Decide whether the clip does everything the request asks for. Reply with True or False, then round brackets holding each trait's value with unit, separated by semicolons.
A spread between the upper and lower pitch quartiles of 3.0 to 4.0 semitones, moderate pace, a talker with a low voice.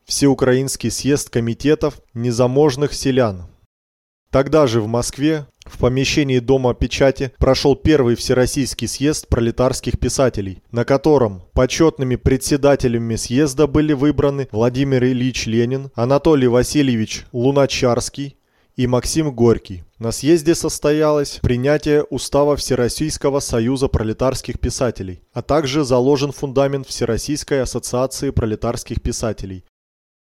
False (3.3 semitones; 105 wpm; 130 Hz)